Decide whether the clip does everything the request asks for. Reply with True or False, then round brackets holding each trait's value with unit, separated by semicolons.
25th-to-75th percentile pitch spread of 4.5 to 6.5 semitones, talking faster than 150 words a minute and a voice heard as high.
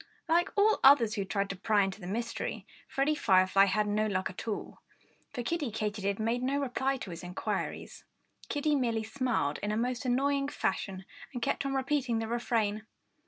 True (5.0 semitones; 180 wpm; 230 Hz)